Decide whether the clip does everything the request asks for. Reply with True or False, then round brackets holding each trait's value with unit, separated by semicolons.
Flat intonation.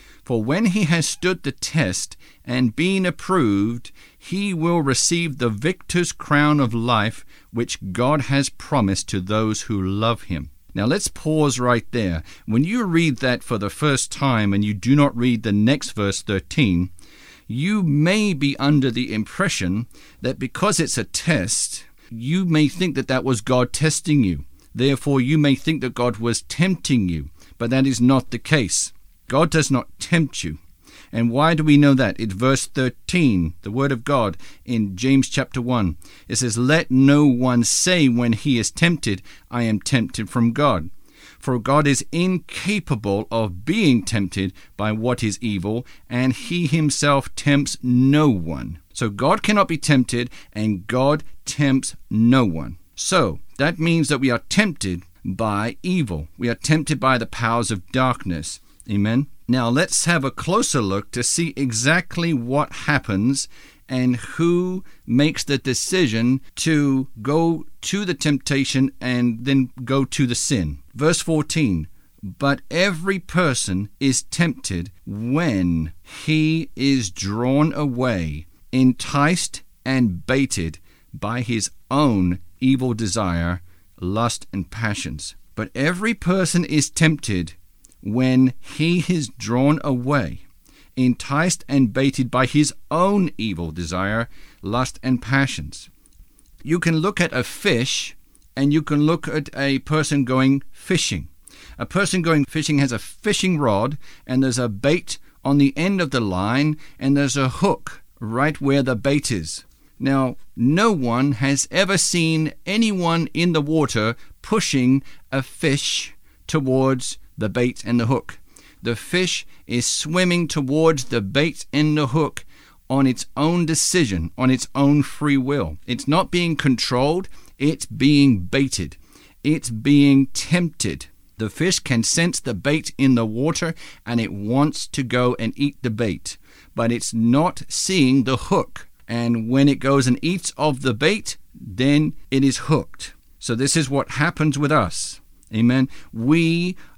False (5.2 semitones)